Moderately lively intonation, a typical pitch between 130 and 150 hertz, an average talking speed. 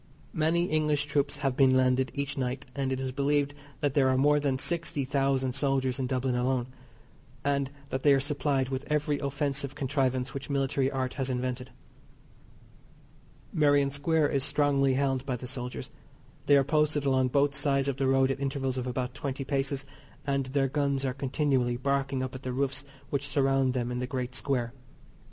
No: narrow, 1.5 semitones; low, 135 Hz; average, 180 wpm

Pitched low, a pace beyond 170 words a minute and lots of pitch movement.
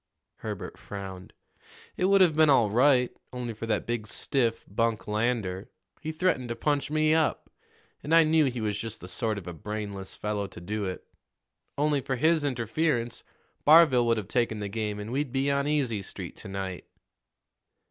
Yes: low, 120 Hz; average, 180 wpm; wide, 5.7 semitones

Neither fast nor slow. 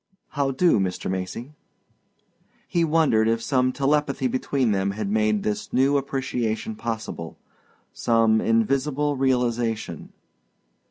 No: slow, 110 wpm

